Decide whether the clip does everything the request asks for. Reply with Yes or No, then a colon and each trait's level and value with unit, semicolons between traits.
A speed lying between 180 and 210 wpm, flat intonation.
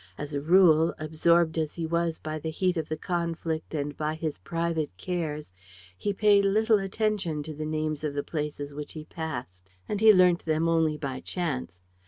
Yes: average, 190 wpm; narrow, 2.3 semitones